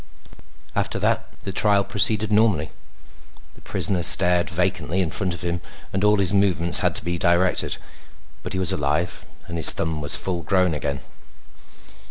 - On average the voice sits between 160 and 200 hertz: No, very low, 90 Hz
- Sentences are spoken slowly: No, average, 165 wpm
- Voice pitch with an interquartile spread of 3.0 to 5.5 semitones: No, narrow, 2.5 semitones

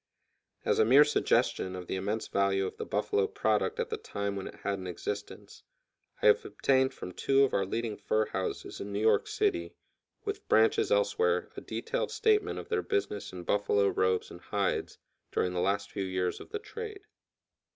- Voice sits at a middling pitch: No, low, 105 Hz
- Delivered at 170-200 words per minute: Yes, average, 190 wpm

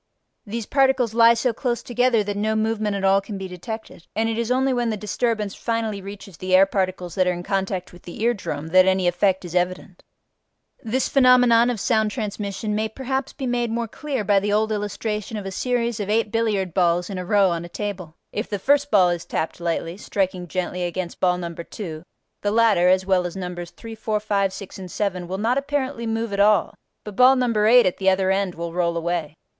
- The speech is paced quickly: Yes, fast, 220 wpm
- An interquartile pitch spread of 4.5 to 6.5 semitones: No, average, 3.8 semitones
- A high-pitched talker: Yes, high, 205 Hz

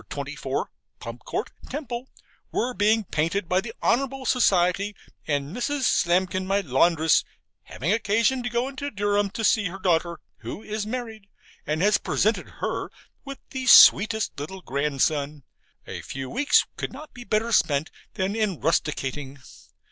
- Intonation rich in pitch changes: Yes, wide, 6.3 semitones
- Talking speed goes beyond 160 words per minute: No, average, 150 wpm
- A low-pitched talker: No, high, 200 Hz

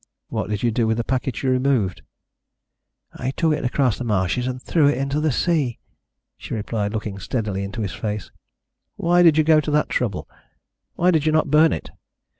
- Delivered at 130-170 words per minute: No, average, 200 wpm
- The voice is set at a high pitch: No, low, 125 Hz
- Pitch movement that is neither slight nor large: No, wide, 5.8 semitones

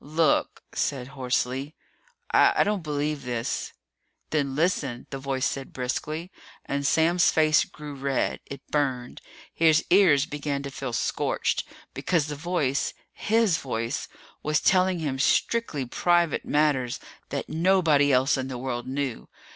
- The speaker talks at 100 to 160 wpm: Yes, slow, 135 wpm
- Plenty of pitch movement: No, average, 3.3 semitones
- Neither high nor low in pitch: Yes, medium, 145 Hz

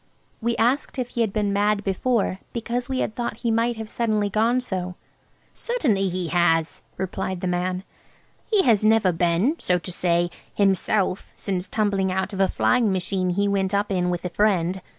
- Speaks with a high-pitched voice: Yes, high, 200 Hz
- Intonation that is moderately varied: Yes, average, 3.5 semitones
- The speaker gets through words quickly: No, average, 185 wpm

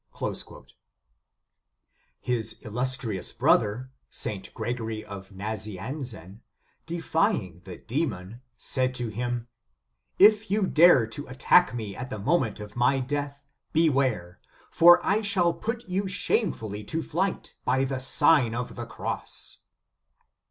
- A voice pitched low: Yes, low, 125 Hz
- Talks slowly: Yes, slow, 120 wpm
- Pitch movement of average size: No, wide, 7.1 semitones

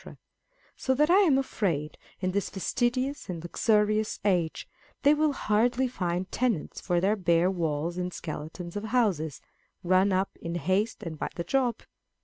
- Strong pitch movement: Yes, wide, 5.9 semitones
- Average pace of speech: Yes, average, 155 wpm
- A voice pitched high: Yes, high, 195 Hz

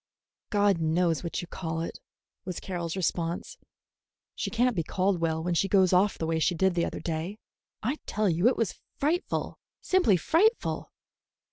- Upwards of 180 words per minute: No, average, 170 wpm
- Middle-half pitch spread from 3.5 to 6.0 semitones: Yes, average, 3.8 semitones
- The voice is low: No, medium, 180 Hz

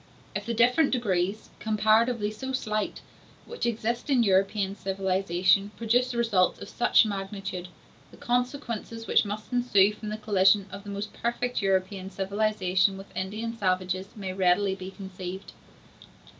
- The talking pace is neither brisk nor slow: No, slow, 130 wpm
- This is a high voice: Yes, high, 205 Hz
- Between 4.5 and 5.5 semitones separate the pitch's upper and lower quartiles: No, average, 3.2 semitones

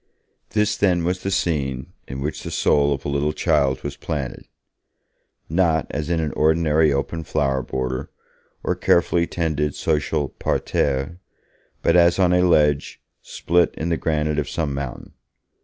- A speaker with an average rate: Yes, average, 155 wpm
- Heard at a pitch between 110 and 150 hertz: No, very low, 75 Hz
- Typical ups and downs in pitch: Yes, average, 3.1 semitones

